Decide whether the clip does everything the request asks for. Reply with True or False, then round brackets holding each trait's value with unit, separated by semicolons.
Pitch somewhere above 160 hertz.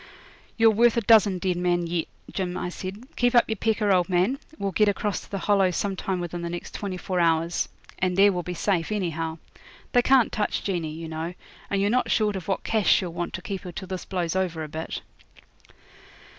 True (185 Hz)